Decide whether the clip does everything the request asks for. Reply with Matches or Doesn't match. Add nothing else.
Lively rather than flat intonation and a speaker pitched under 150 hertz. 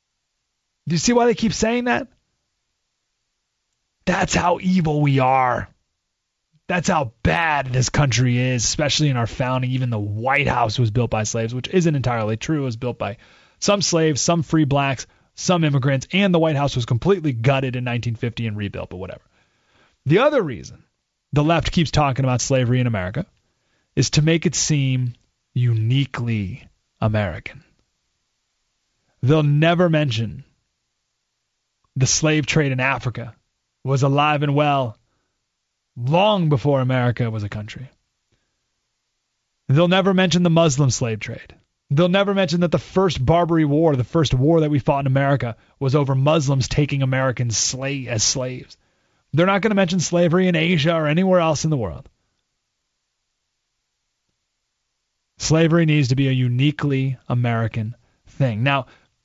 Doesn't match